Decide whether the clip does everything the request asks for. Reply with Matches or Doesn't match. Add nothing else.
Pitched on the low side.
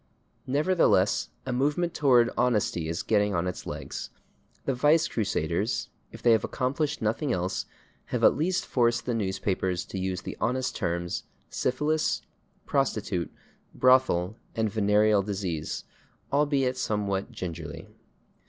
Matches